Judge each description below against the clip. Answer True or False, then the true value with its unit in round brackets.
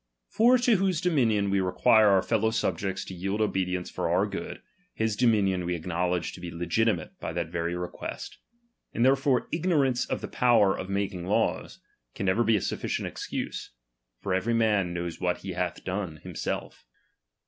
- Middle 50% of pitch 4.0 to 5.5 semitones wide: True (4.4 semitones)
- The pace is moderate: True (170 wpm)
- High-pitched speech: False (100 Hz)